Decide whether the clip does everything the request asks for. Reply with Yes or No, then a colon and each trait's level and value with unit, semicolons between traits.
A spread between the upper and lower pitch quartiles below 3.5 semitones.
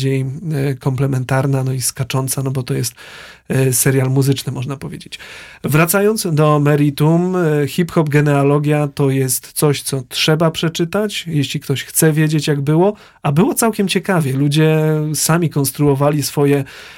Yes: narrow, 2.6 semitones